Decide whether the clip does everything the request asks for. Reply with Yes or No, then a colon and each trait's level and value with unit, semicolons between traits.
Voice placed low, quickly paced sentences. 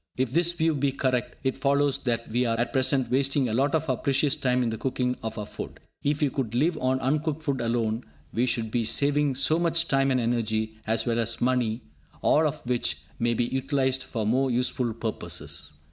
Yes: low, 130 Hz; fast, 210 wpm